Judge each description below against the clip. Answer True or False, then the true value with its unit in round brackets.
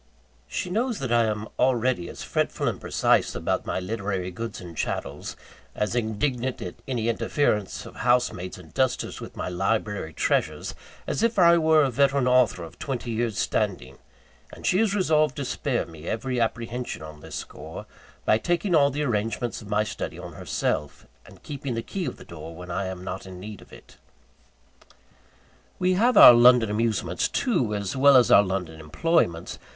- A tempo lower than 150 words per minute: False (180 wpm)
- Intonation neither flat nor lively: False (6.4 semitones)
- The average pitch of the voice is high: False (115 Hz)